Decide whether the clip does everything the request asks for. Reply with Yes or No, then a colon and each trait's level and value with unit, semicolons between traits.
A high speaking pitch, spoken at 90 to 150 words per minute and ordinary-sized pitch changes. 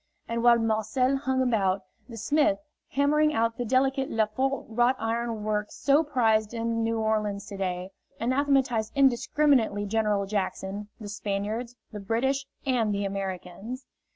Yes: high, 225 Hz; average, 140 wpm; average, 3.9 semitones